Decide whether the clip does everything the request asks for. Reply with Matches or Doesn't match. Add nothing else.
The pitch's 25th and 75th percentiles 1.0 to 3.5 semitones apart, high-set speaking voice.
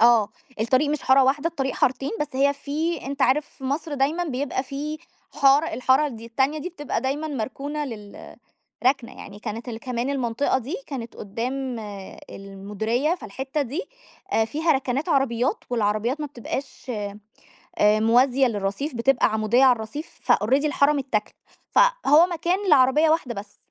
Doesn't match